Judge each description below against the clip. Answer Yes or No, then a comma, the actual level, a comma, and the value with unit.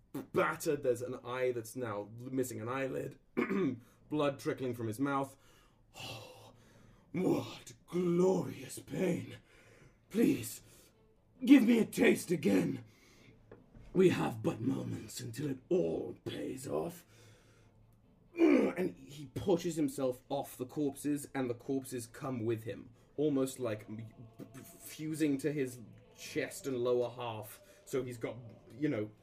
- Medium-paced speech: No, slow, 125 wpm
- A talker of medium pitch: No, low, 125 Hz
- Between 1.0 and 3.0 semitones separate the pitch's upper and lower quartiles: No, average, 3.8 semitones